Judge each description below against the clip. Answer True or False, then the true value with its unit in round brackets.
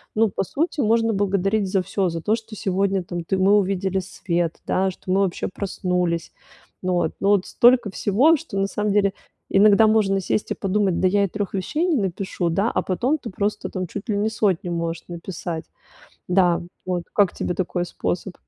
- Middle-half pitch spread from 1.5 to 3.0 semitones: True (2.6 semitones)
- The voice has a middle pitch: False (195 Hz)